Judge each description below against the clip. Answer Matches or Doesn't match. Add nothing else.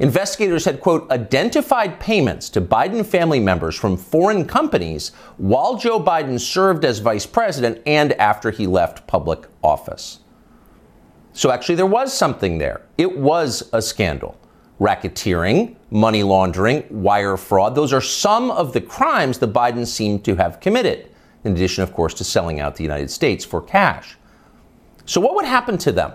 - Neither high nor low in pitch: Doesn't match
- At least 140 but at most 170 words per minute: Matches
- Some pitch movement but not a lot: Doesn't match